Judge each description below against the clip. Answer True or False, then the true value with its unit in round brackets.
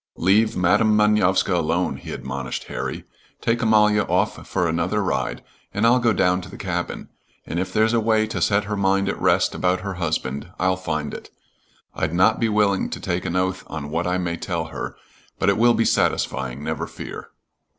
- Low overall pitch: True (95 Hz)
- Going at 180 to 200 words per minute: True (195 wpm)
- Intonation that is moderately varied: True (3.7 semitones)